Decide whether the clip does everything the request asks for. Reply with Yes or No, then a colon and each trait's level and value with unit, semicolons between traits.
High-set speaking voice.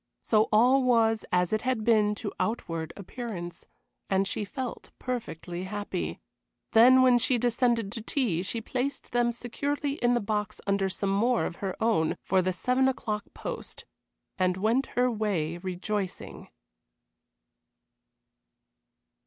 Yes: high, 220 Hz